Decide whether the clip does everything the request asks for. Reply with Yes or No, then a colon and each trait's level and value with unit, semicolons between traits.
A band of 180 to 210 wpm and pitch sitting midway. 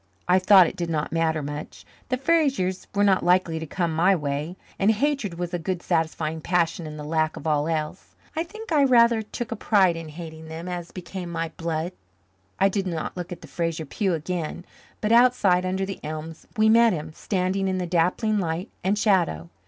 Yes: fast, 205 wpm; medium, 180 Hz